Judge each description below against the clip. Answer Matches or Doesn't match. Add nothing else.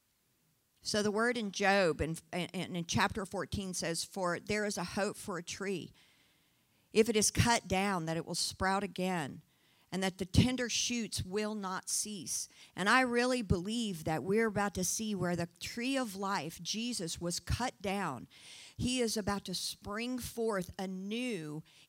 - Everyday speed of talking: Matches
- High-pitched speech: Matches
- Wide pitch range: Doesn't match